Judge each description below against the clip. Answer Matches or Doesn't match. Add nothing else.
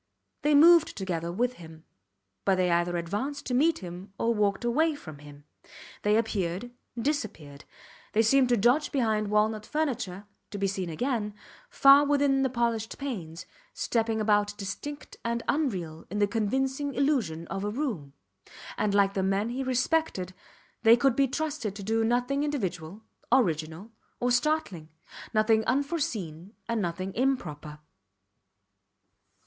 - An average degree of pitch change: Doesn't match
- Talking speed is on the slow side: Doesn't match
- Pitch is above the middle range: Matches